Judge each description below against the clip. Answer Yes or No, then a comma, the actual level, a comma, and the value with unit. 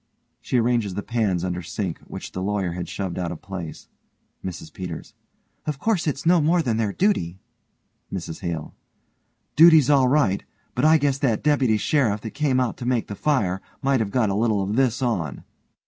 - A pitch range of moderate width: No, wide, 6.7 semitones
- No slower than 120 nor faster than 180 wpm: No, average, 190 wpm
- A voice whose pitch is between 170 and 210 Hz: No, low, 110 Hz